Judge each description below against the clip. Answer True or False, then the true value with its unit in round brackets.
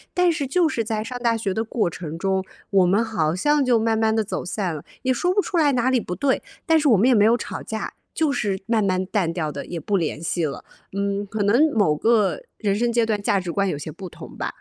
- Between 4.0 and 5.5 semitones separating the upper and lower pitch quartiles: True (4.5 semitones)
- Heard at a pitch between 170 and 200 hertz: False (215 Hz)